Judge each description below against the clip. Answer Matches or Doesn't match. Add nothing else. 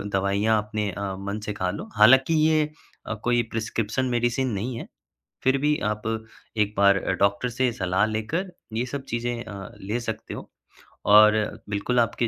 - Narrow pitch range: Doesn't match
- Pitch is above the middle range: Doesn't match